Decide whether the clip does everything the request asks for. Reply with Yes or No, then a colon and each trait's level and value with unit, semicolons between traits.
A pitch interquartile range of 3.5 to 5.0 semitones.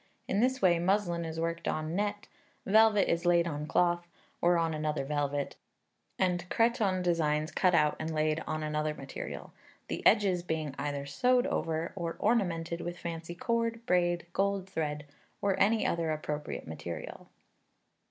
Yes: average, 3.8 semitones